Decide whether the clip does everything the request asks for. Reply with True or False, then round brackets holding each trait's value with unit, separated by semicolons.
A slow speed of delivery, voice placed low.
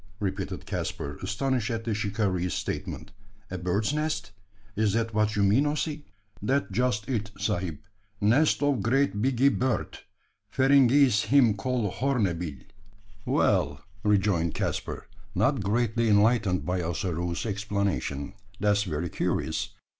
True (125 wpm; 105 Hz)